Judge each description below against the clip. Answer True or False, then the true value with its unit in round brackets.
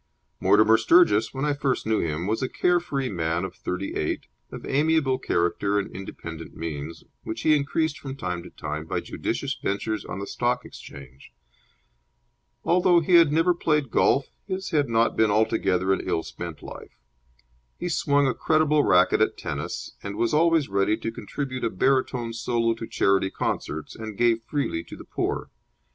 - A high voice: False (115 Hz)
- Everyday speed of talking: True (170 wpm)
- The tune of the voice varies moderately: False (6.9 semitones)